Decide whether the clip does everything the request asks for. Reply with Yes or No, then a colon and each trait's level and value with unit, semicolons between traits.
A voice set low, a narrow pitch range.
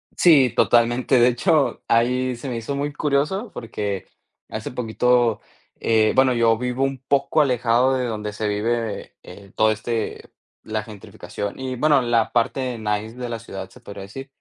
No: low, 120 Hz; average, 3.1 semitones